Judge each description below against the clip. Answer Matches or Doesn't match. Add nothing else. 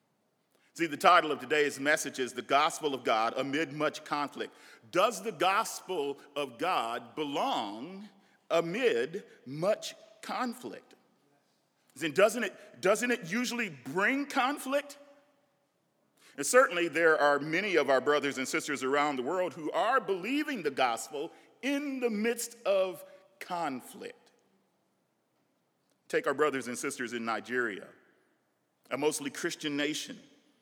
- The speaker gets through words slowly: Matches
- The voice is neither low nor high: Matches